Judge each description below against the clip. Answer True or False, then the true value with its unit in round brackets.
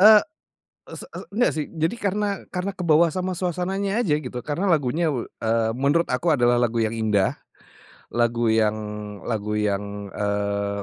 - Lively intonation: True (8.7 semitones)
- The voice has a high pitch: False (130 Hz)